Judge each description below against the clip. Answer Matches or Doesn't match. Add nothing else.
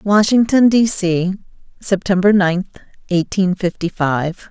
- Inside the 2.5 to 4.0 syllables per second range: Matches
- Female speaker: Matches